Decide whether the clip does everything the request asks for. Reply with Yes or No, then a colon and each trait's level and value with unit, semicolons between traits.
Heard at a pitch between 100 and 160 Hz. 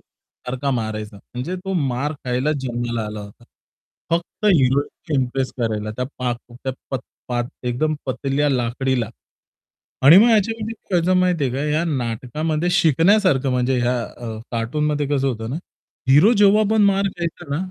Yes: low, 135 Hz